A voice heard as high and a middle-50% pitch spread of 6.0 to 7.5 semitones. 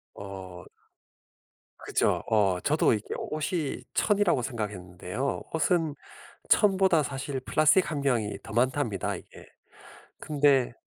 No: low, 135 Hz; wide, 6.7 semitones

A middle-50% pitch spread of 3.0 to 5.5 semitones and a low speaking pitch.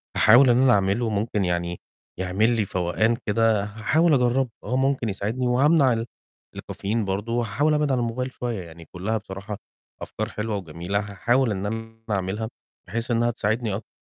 Yes: average, 3.5 semitones; low, 110 Hz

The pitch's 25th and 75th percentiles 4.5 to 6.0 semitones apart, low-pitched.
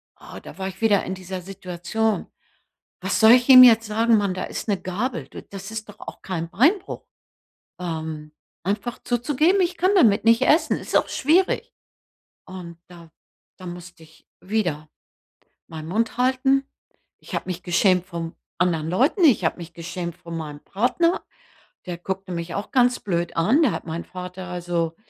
No: average, 5.2 semitones; high, 190 Hz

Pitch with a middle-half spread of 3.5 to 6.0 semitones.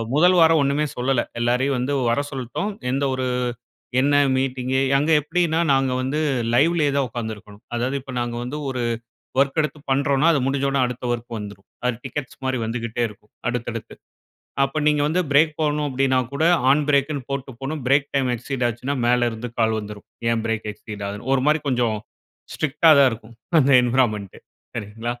No: average, 3.1 semitones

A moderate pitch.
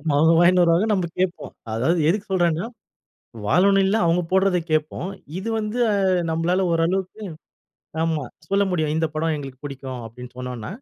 Yes: medium, 170 Hz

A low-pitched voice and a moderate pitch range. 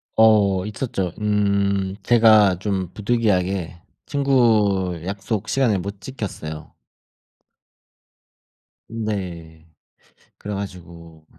Yes: low, 100 Hz; average, 3.1 semitones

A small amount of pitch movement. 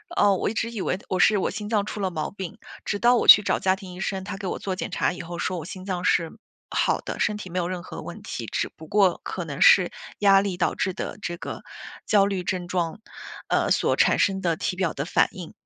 Yes: narrow, 2.3 semitones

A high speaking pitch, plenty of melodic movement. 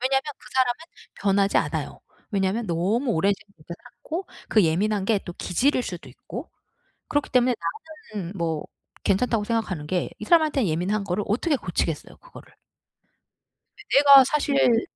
Yes: high, 215 Hz; wide, 5.8 semitones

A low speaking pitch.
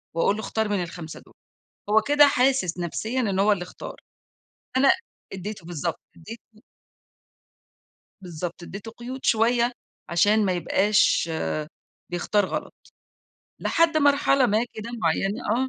No: high, 210 Hz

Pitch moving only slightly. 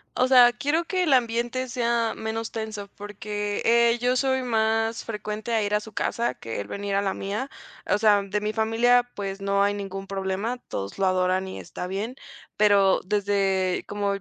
No: average, 3.0 semitones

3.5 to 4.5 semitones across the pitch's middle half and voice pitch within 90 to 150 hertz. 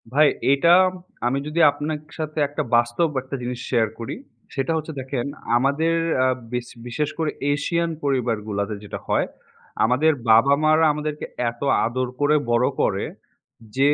Yes: average, 4.1 semitones; medium, 140 Hz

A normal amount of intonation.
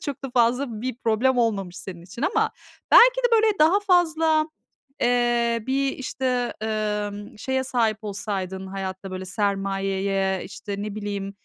Yes: average, 5.0 semitones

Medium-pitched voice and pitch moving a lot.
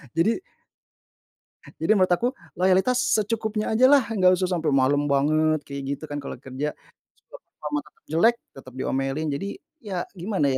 Yes: medium, 165 Hz; wide, 6.5 semitones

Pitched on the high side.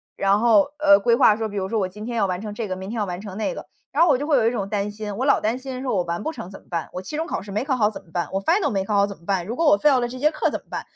Yes: high, 210 Hz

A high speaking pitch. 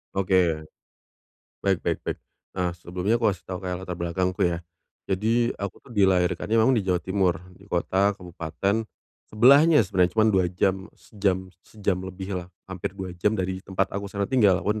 No: very low, 95 Hz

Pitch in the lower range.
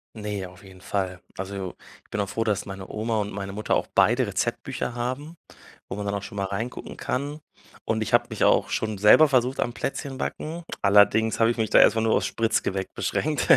Yes: low, 105 Hz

